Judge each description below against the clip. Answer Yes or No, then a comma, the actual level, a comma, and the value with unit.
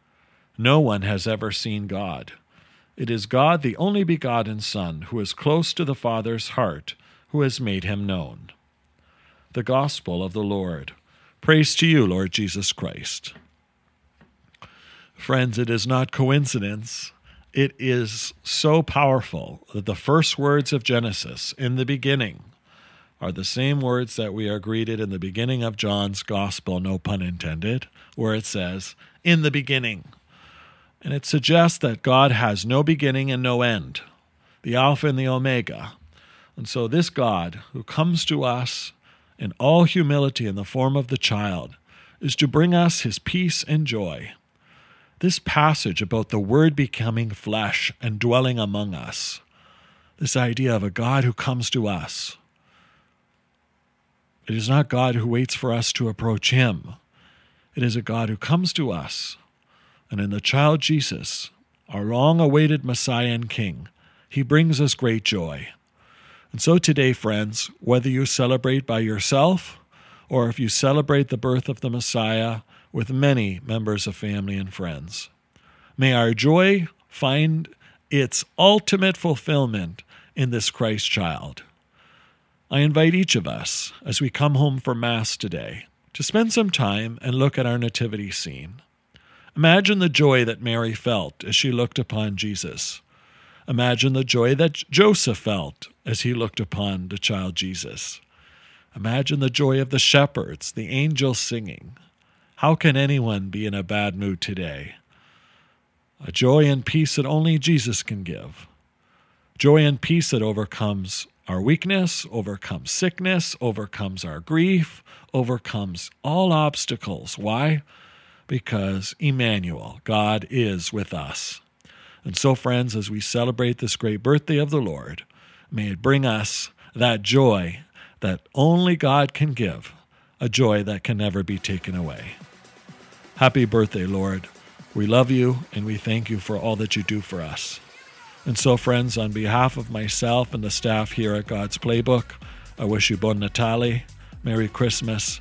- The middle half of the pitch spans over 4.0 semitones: Yes, average, 4.9 semitones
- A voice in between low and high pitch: No, low, 120 Hz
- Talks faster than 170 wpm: No, average, 155 wpm